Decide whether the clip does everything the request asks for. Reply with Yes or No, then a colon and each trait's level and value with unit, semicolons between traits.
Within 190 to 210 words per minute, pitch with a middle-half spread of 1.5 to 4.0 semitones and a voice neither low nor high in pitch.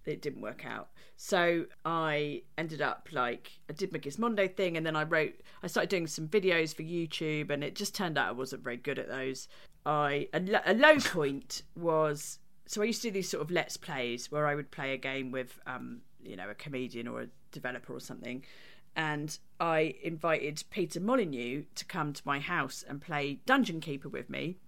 Yes: fast, 205 wpm; average, 3.6 semitones; medium, 155 Hz